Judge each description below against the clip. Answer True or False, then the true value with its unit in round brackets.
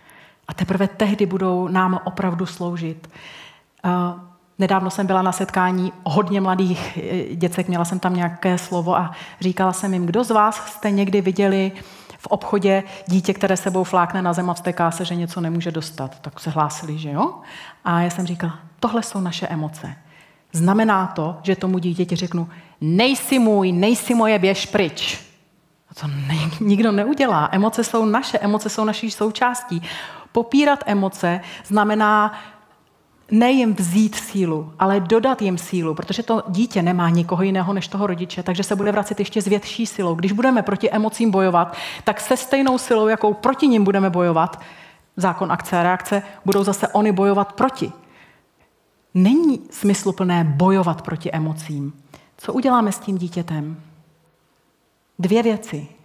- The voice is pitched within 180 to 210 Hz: True (190 Hz)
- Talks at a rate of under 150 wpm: False (155 wpm)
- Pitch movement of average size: True (3.3 semitones)